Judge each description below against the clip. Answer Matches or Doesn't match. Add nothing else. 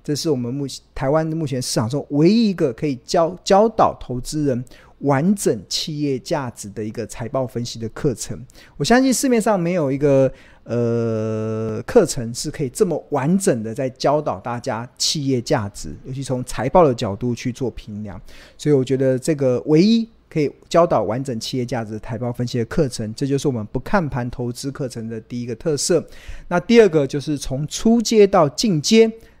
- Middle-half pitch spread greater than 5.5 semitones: Doesn't match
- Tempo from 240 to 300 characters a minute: Matches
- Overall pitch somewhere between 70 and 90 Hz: Doesn't match